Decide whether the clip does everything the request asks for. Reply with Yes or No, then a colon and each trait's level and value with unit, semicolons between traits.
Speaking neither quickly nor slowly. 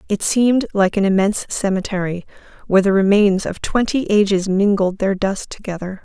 Yes: average, 160 wpm